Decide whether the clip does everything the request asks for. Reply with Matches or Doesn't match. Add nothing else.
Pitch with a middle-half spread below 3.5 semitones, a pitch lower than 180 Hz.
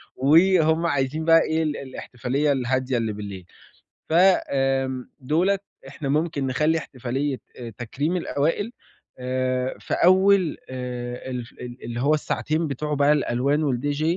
Doesn't match